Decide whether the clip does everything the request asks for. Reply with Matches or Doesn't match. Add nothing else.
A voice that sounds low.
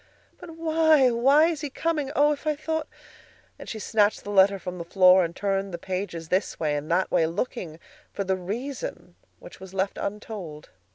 Doesn't match